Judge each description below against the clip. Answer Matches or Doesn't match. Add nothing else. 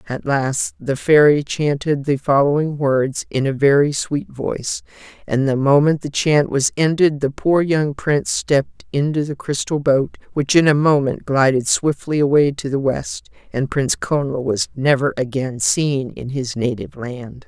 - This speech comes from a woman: Matches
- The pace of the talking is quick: Doesn't match